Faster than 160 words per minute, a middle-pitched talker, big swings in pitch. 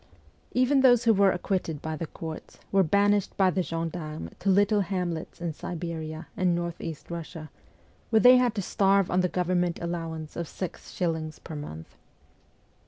No: average, 170 wpm; medium, 175 Hz; average, 3.5 semitones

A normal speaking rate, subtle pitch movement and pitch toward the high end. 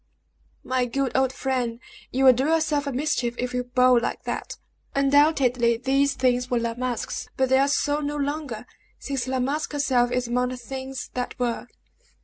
Yes: average, 180 wpm; narrow, 2.1 semitones; very high, 255 Hz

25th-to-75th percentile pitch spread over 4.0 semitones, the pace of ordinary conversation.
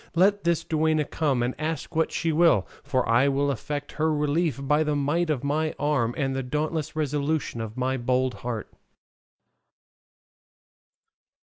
No: average, 3.2 semitones; average, 150 wpm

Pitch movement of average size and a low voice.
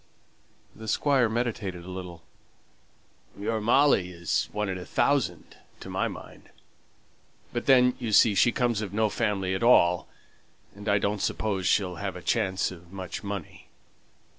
Yes: average, 3.8 semitones; low, 100 Hz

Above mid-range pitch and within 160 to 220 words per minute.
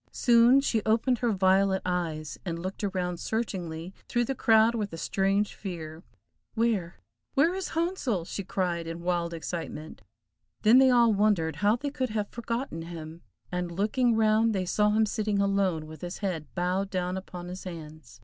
Yes: high, 195 Hz; average, 170 wpm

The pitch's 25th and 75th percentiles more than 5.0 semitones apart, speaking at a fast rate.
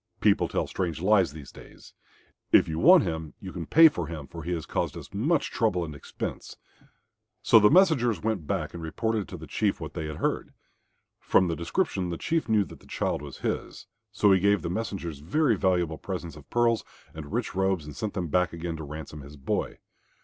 Yes: wide, 5.4 semitones; fast, 210 wpm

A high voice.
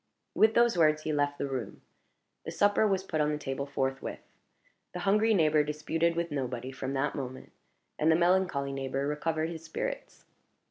No: medium, 155 Hz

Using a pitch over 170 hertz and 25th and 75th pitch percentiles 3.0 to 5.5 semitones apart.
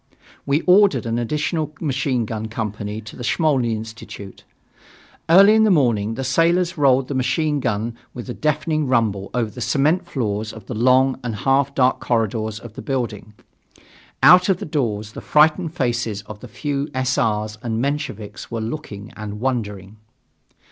No: low, 125 Hz; average, 5.2 semitones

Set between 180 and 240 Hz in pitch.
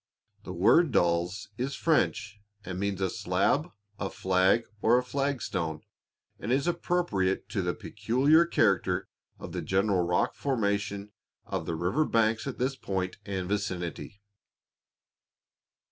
No: low, 100 Hz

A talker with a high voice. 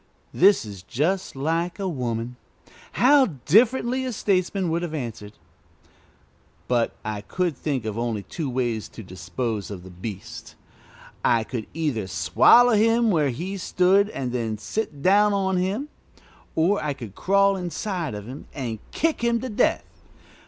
No: medium, 155 Hz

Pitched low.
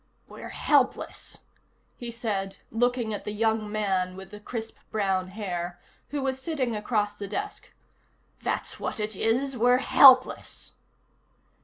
No: high, 220 Hz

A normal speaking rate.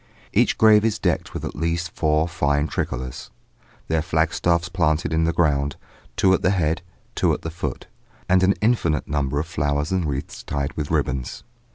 Yes: average, 180 wpm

